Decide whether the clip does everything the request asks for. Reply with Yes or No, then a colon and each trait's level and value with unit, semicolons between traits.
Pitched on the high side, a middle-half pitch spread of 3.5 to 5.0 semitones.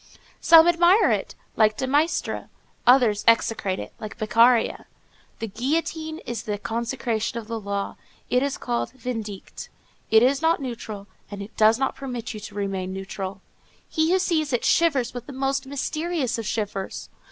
Yes: high, 240 Hz; average, 4.5 semitones